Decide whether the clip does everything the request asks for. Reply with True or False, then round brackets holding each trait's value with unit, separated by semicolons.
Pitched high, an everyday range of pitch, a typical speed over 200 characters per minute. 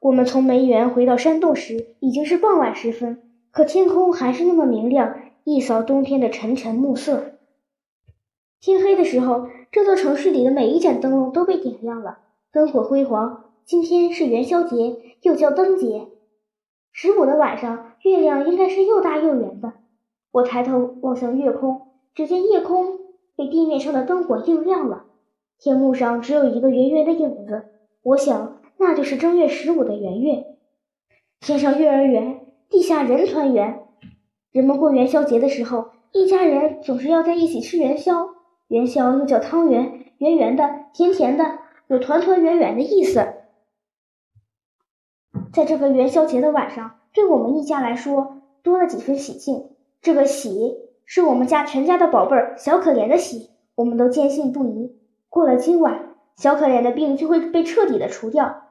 True (280 Hz; 5.0 semitones; 250 characters per minute)